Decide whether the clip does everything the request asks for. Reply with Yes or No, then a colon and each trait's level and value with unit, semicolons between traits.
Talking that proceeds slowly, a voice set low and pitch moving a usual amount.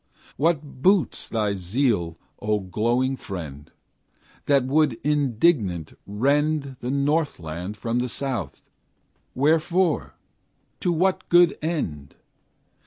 No: slow, 100 wpm; low, 130 Hz; wide, 6.9 semitones